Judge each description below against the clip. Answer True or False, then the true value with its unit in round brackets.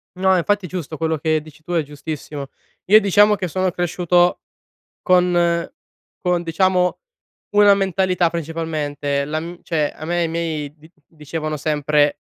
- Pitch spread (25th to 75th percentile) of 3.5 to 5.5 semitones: False (2.8 semitones)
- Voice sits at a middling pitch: True (165 Hz)